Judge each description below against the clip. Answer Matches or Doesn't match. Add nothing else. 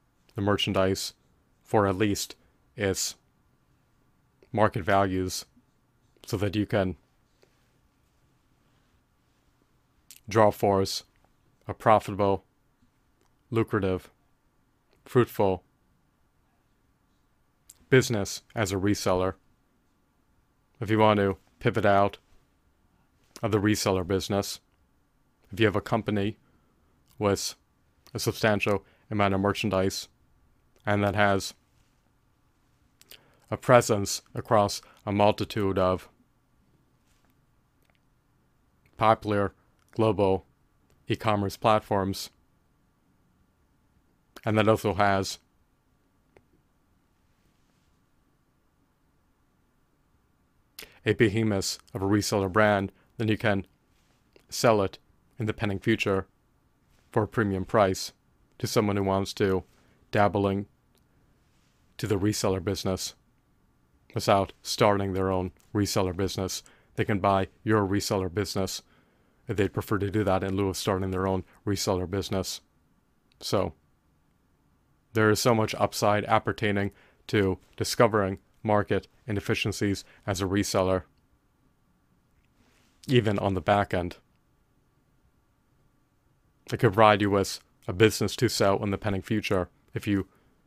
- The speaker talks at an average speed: Doesn't match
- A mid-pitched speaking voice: Doesn't match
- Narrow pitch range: Matches